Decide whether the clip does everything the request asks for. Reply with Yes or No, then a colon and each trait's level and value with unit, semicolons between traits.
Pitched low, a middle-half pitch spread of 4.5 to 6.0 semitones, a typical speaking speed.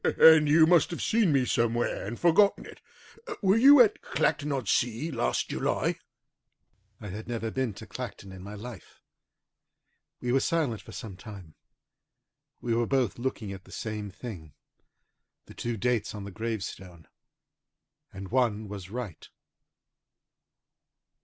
Yes: low, 115 Hz; average, 5.1 semitones; average, 145 wpm